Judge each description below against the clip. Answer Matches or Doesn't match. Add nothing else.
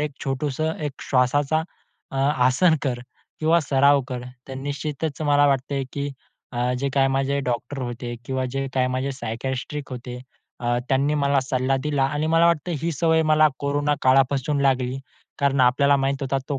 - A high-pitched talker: Doesn't match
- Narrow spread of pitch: Matches